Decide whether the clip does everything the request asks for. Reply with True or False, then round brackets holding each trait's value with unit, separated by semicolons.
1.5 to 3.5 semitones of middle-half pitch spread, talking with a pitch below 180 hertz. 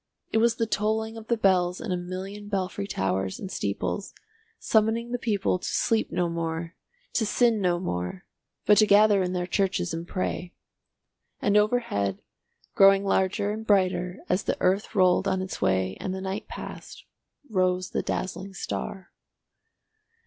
False (2.8 semitones; 190 Hz)